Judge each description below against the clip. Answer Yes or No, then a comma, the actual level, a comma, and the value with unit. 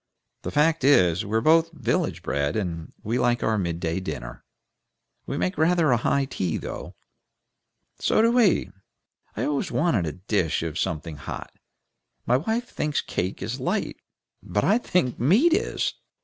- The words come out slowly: No, average, 160 wpm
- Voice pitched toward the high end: No, low, 120 Hz